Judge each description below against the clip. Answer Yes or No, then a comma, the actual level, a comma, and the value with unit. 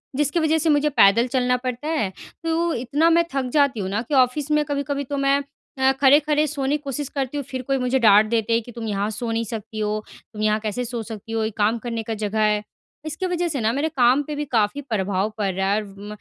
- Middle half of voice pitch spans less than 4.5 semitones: No, average, 5.0 semitones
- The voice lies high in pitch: Yes, very high, 250 Hz